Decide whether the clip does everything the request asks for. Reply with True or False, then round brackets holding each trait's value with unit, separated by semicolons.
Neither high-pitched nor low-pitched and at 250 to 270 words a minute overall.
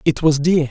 True (155 Hz; 255 wpm)